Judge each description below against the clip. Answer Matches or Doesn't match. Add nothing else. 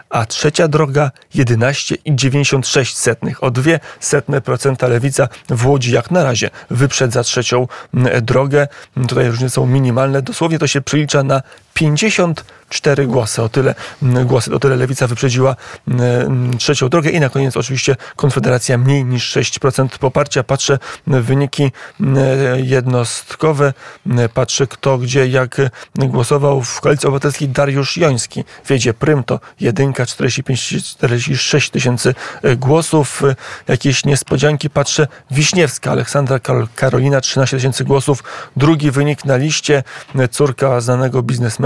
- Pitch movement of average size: Doesn't match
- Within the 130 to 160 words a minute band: Doesn't match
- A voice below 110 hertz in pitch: Doesn't match